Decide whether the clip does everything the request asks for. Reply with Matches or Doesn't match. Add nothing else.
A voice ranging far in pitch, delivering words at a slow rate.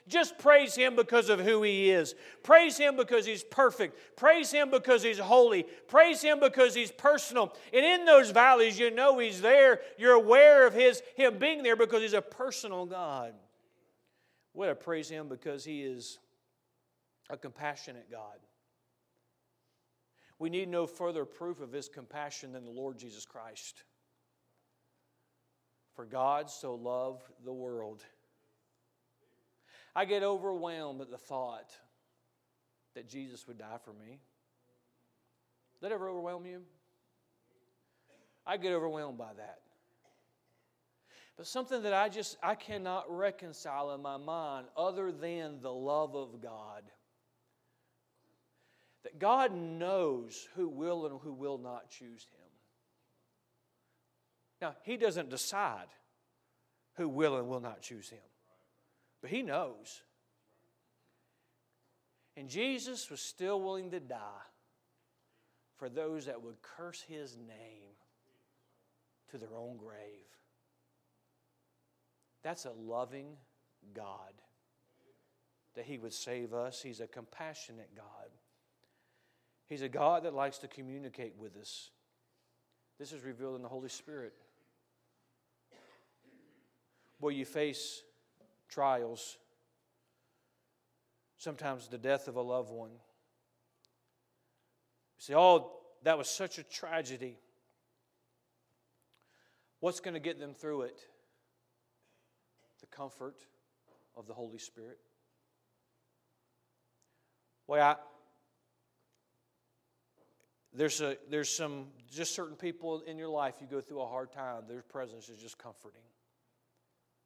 Matches